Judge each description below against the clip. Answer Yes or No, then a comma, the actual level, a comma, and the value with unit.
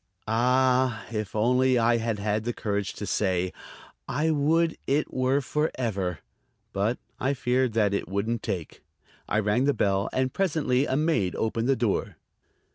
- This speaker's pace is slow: No, average, 160 wpm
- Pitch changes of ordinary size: Yes, average, 4.0 semitones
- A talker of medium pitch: No, low, 120 Hz